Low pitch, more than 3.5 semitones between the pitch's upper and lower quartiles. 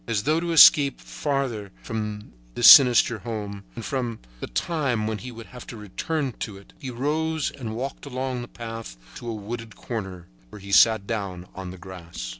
Yes: low, 115 Hz; average, 4.5 semitones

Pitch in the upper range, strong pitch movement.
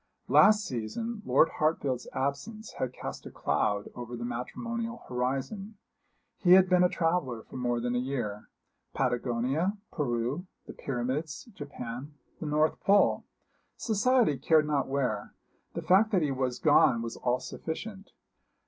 No: medium, 140 Hz; wide, 7.1 semitones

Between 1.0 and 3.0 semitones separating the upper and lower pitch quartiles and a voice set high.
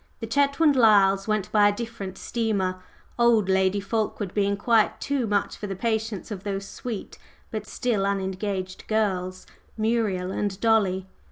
Yes: average, 2.7 semitones; high, 205 Hz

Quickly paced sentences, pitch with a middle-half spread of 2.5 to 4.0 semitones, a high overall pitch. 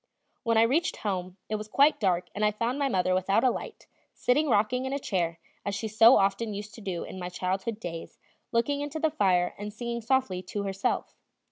No: fast, 215 wpm; average, 4.6 semitones; high, 210 Hz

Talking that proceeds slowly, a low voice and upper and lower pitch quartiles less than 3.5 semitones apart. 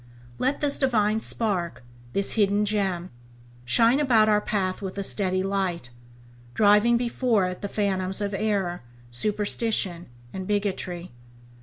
No: slow, 130 wpm; high, 205 Hz; narrow, 2.6 semitones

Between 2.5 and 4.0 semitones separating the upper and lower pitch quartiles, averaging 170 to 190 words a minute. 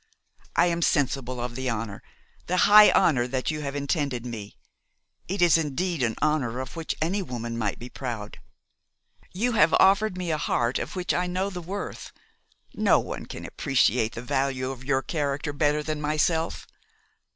No: wide, 5.5 semitones; average, 175 wpm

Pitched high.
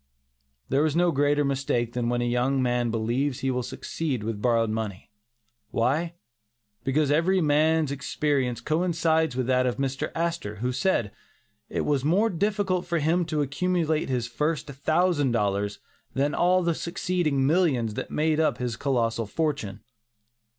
No: medium, 140 Hz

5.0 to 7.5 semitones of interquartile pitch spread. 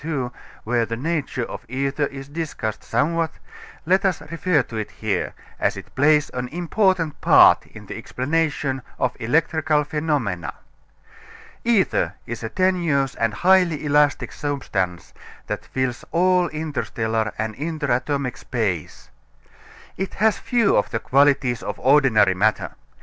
Yes: average, 5.3 semitones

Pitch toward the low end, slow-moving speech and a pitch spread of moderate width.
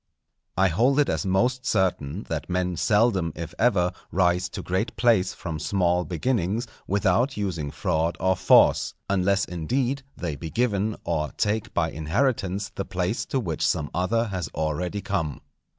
No: very low, 95 Hz; average, 160 wpm; average, 4.2 semitones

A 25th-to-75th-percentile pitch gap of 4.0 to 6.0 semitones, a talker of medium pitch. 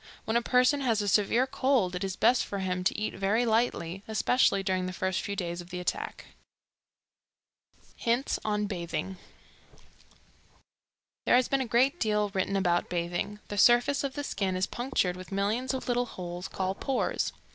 No: average, 4.8 semitones; high, 205 Hz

